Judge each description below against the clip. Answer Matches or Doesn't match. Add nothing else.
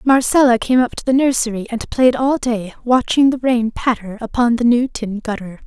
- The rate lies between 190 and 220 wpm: Matches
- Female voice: Matches